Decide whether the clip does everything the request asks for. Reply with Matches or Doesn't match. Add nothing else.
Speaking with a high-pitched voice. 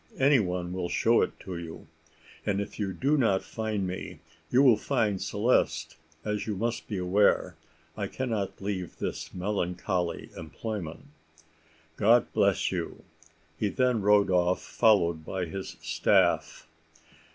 Doesn't match